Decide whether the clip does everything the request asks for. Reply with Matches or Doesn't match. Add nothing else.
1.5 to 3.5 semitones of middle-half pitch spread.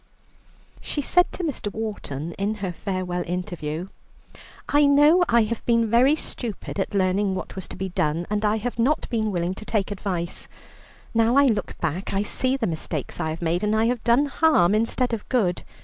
Doesn't match